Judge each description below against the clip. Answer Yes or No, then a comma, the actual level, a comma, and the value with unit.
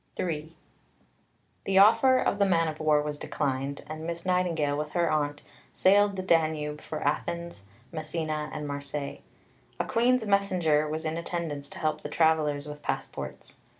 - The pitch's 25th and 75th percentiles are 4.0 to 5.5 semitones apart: No, average, 2.8 semitones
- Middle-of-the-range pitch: Yes, medium, 155 Hz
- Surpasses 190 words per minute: No, average, 160 wpm